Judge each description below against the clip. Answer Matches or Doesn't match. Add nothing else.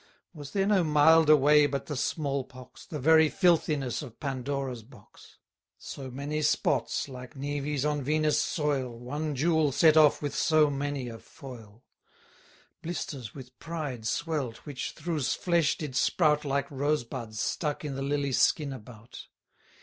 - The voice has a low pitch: Doesn't match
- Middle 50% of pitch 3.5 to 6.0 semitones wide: Doesn't match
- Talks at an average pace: Matches